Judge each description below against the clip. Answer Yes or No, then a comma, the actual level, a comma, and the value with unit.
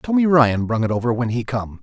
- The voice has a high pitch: No, low, 125 Hz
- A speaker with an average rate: No, fast, 260 wpm